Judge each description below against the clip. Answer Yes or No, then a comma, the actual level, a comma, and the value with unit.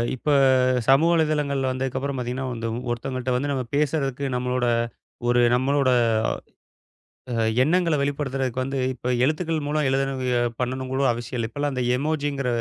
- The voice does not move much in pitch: Yes, narrow, 2.2 semitones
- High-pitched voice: No, low, 135 Hz